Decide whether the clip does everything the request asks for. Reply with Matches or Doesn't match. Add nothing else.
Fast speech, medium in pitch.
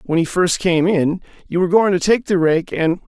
Matches